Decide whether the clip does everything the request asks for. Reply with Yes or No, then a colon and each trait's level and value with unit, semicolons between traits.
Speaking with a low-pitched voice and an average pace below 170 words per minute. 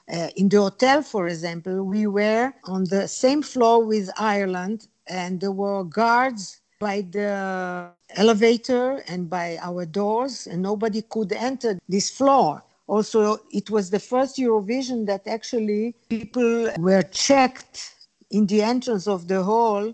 No: high, 210 Hz; average, 145 wpm